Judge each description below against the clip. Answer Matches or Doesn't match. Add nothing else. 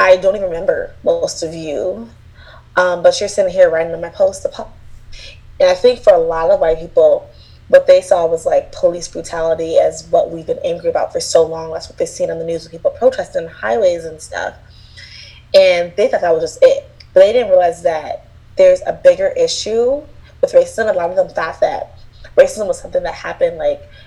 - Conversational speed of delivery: Doesn't match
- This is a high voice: Matches